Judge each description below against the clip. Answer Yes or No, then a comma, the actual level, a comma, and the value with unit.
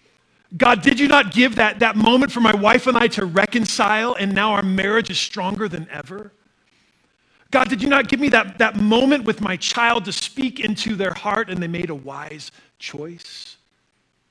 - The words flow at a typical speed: Yes, average, 195 wpm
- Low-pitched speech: No, high, 220 Hz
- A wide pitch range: No, average, 3.9 semitones